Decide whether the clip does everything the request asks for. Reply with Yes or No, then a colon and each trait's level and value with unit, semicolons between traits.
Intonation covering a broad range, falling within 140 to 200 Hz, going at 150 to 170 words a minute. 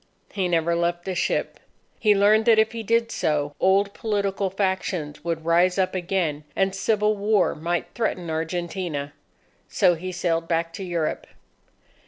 No: average, 3.2 semitones; medium, 185 Hz; average, 155 wpm